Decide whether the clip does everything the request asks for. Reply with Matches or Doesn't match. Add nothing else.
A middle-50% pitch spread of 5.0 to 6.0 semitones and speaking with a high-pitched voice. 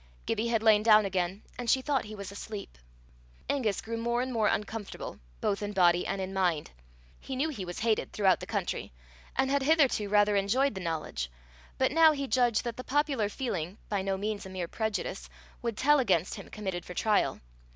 Doesn't match